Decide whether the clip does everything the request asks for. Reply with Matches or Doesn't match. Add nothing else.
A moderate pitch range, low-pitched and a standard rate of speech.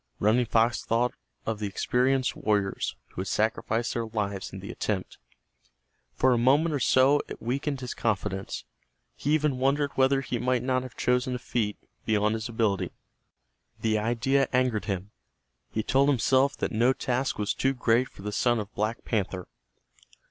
Matches